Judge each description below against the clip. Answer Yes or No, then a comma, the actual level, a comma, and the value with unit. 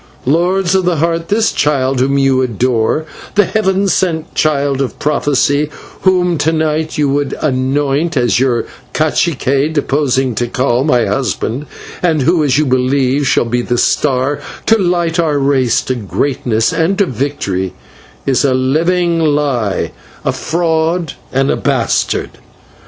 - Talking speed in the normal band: Yes, average, 145 wpm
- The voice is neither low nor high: Yes, medium, 145 Hz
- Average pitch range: Yes, average, 4.1 semitones